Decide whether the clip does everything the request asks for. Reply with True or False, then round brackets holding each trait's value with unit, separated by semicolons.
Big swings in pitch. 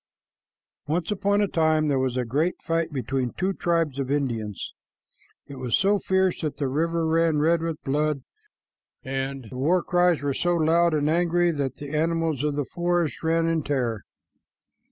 False (3.7 semitones)